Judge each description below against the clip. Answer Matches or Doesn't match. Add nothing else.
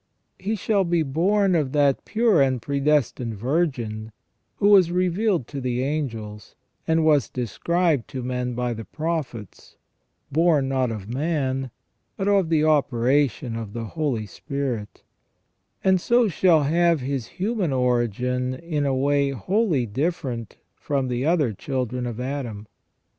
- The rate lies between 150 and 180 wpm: Doesn't match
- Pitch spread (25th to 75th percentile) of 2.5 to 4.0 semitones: Doesn't match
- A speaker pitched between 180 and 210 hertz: Doesn't match